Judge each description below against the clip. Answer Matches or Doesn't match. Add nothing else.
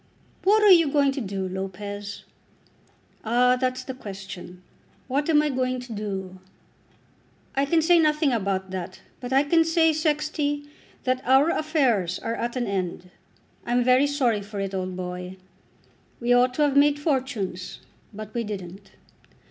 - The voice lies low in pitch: Doesn't match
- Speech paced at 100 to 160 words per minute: Matches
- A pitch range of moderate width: Doesn't match